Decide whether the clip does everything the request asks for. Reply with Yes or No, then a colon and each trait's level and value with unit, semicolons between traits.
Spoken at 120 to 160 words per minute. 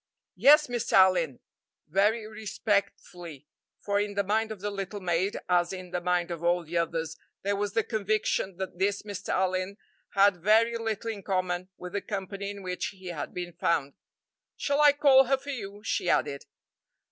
No: average, 180 wpm